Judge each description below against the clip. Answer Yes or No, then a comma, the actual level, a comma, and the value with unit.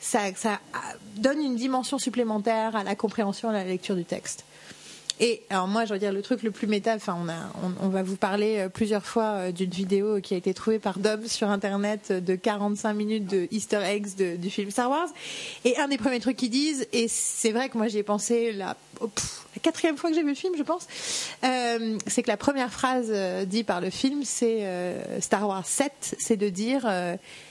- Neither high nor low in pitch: No, high, 215 Hz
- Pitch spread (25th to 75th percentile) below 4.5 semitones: Yes, average, 3.4 semitones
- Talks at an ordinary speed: No, fast, 225 wpm